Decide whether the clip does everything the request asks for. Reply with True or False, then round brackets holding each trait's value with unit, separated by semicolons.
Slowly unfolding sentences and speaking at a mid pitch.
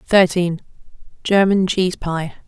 True (75 wpm; 180 Hz)